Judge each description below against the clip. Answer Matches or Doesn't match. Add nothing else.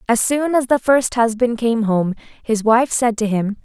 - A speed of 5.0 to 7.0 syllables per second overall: Doesn't match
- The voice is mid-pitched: Doesn't match